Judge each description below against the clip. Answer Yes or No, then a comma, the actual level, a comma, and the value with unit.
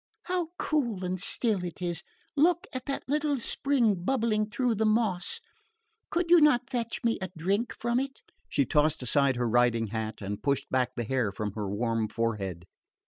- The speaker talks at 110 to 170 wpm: No, average, 180 wpm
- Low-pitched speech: No, medium, 185 Hz